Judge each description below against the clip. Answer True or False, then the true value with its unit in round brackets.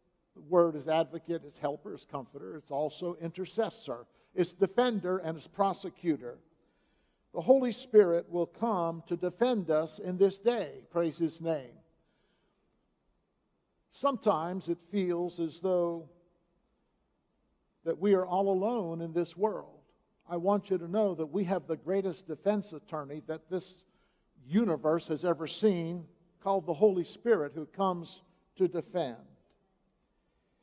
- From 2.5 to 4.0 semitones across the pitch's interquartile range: True (3.1 semitones)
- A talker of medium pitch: True (175 Hz)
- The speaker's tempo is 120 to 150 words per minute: True (135 wpm)